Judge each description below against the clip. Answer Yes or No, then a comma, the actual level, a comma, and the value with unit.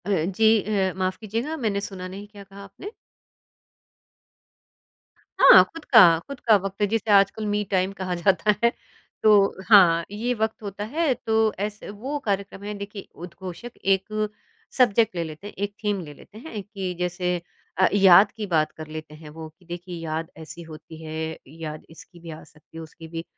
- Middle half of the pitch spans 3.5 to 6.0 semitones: Yes, average, 3.9 semitones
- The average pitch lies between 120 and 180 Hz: No, high, 195 Hz